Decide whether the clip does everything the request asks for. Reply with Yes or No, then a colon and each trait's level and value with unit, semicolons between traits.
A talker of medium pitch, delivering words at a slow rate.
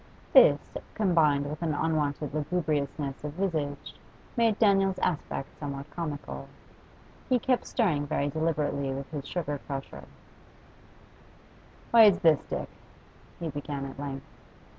Yes: medium, 150 Hz; slow, 120 wpm